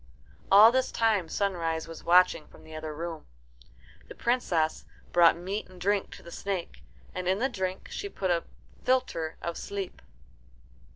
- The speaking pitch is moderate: Yes, medium, 180 Hz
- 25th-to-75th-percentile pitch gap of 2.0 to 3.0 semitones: No, average, 3.4 semitones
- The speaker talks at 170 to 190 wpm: No, average, 160 wpm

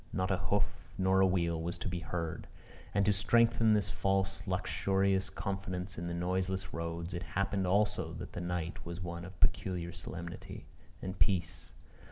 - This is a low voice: Yes, very low, 95 Hz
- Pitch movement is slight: Yes, narrow, 2.1 semitones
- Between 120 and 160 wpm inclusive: No, average, 170 wpm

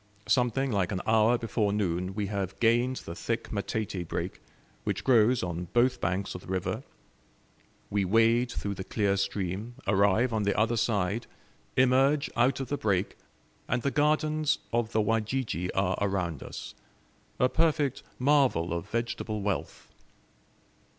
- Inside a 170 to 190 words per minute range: No, average, 150 wpm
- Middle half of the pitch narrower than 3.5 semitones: No, average, 4.2 semitones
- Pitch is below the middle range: Yes, low, 110 Hz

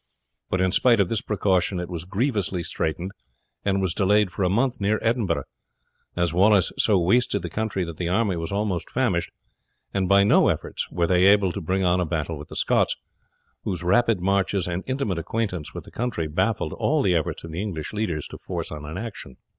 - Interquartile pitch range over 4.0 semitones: No, average, 3.4 semitones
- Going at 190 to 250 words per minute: Yes, fast, 205 wpm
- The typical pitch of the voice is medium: No, very low, 95 Hz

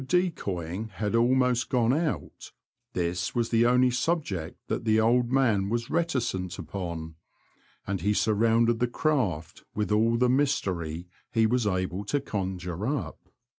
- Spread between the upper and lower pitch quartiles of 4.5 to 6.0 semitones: Yes, average, 5.2 semitones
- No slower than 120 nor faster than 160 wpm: Yes, average, 140 wpm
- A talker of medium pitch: No, low, 110 Hz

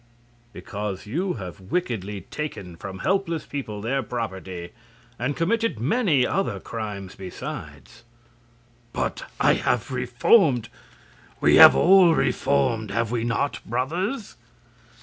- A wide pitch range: Yes, wide, 7.7 semitones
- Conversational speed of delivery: No, slow, 110 wpm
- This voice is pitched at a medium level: No, low, 120 Hz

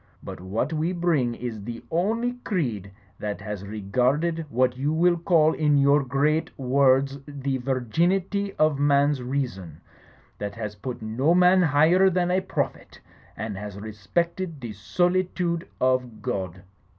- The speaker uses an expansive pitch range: Yes, wide, 6.8 semitones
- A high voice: No, medium, 140 Hz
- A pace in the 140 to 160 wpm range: Yes, average, 150 wpm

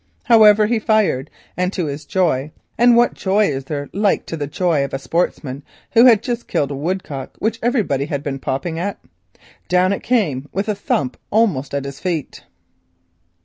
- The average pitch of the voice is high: No, medium, 175 Hz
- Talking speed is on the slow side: No, average, 185 wpm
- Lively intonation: Yes, wide, 7.1 semitones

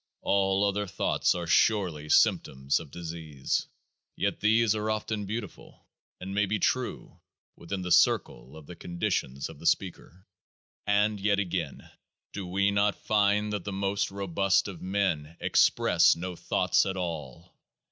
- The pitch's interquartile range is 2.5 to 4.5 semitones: Yes, average, 3.3 semitones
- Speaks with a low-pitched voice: Yes, very low, 95 Hz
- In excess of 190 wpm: No, average, 145 wpm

